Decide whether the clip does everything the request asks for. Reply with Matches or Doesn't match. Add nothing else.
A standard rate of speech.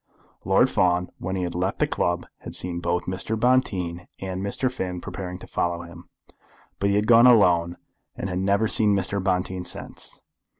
Matches